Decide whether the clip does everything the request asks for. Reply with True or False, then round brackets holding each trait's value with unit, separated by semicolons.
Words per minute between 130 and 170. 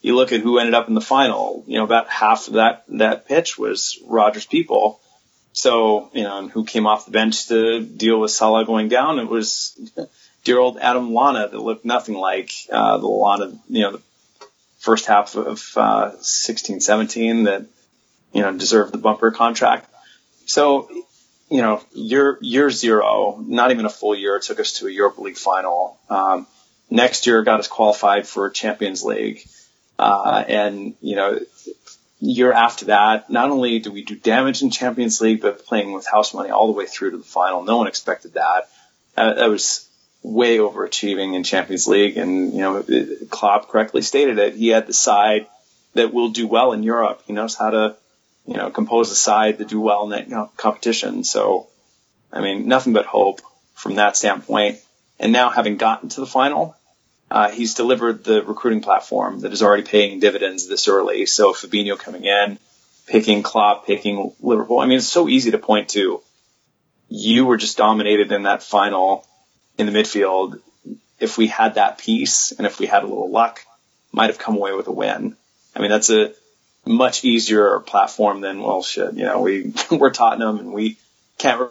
False (190 wpm)